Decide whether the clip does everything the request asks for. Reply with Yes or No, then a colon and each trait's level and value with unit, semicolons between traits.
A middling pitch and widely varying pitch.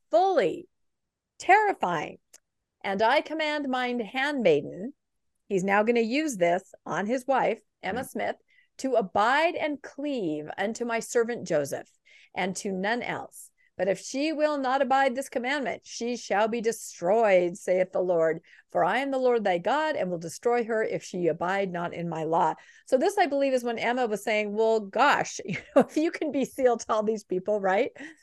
No: high, 240 Hz; wide, 6.6 semitones